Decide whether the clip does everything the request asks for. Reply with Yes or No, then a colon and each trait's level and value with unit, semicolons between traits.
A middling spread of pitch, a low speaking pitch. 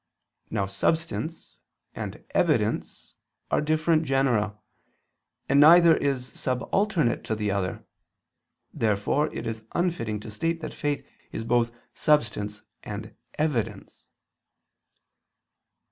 No: wide, 6.5 semitones; low, 130 Hz